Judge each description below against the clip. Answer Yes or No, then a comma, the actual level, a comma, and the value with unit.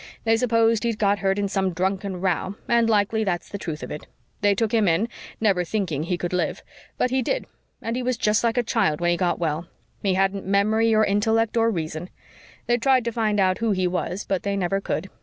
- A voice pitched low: No, high, 200 Hz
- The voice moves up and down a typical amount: Yes, average, 3.6 semitones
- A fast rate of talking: Yes, fast, 230 wpm